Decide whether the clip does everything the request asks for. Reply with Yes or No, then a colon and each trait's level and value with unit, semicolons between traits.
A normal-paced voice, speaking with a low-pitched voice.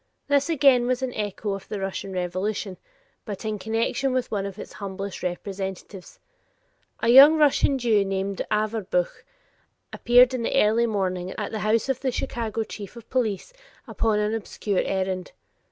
No: average, 160 wpm; high, 215 Hz